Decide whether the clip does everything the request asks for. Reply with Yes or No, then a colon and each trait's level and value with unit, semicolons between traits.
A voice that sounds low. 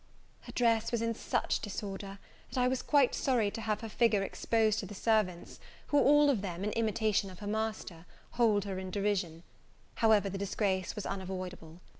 No: high, 210 Hz